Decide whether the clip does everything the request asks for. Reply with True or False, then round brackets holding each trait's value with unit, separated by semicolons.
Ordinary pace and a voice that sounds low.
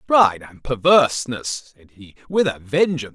True (155 wpm; 125 Hz)